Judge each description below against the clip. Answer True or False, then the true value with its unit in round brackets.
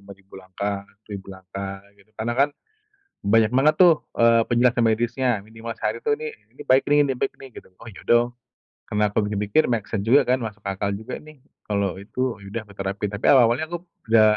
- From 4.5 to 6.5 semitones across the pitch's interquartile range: False (4.0 semitones)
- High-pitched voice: False (115 Hz)